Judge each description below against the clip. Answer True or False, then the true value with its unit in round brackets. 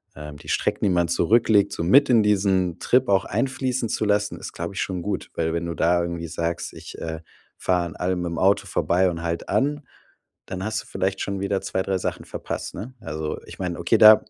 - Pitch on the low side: True (95 Hz)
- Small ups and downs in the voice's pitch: False (3.5 semitones)